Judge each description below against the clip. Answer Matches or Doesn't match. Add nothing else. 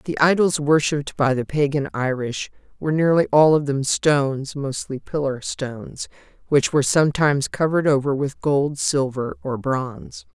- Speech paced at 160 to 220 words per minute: Doesn't match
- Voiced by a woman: Matches